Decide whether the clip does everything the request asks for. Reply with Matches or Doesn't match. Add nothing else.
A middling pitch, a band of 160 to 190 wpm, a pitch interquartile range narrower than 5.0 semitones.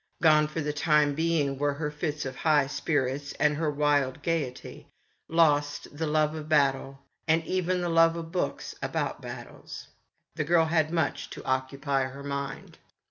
Matches